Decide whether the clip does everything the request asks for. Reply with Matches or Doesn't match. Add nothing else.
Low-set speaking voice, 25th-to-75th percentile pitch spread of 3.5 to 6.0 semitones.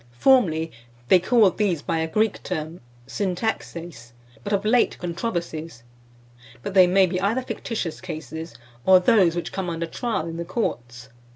Doesn't match